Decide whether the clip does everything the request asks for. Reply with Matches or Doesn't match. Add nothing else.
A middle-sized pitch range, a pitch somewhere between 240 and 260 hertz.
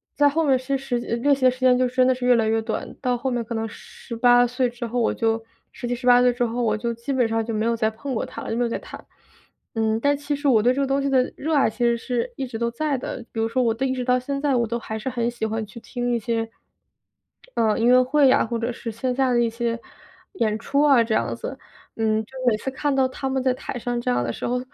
Doesn't match